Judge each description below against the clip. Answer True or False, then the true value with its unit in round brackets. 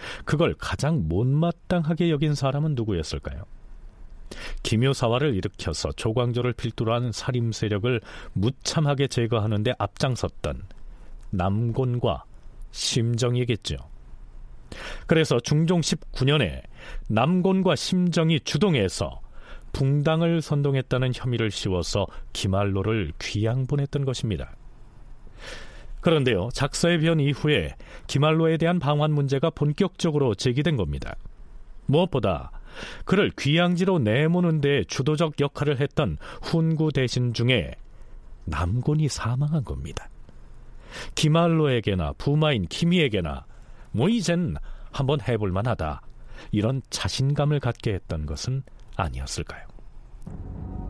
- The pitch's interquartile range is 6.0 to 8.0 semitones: True (7.0 semitones)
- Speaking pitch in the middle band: False (125 Hz)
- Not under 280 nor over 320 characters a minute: False (260 characters per minute)